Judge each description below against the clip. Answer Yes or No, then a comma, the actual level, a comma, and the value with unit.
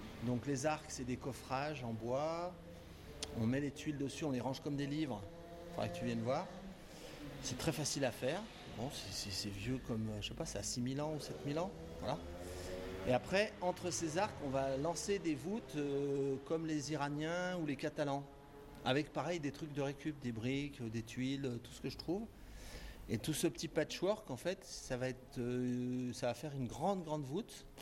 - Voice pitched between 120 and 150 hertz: Yes, medium, 140 Hz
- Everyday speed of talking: Yes, average, 210 wpm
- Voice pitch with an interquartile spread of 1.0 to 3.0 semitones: No, average, 4.3 semitones